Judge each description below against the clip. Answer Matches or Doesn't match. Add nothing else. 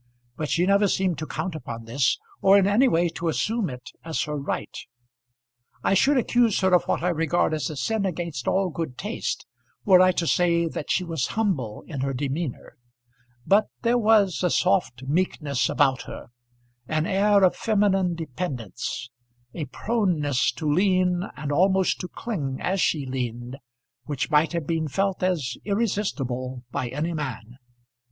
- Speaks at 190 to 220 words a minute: Doesn't match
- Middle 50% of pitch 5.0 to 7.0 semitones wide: Matches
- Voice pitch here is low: Doesn't match